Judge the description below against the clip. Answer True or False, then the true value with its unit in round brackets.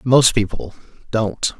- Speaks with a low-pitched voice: True (110 Hz)